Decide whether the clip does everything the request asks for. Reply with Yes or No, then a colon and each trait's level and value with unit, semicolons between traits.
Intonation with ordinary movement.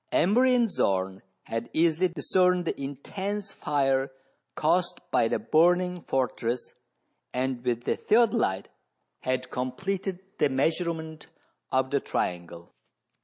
No: wide, 6.2 semitones